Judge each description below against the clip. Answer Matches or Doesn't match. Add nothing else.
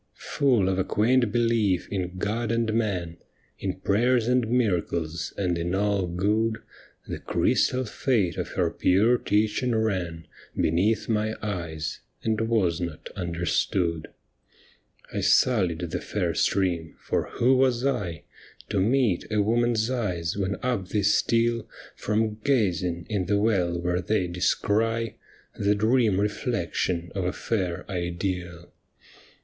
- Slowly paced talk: Matches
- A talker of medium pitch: Doesn't match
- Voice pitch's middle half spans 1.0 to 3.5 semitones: Doesn't match